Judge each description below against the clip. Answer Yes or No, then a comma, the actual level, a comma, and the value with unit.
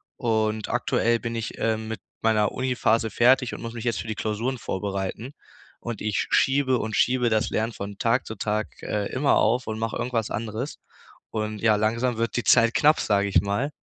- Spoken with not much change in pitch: Yes, narrow, 1.9 semitones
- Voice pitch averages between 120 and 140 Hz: No, low, 110 Hz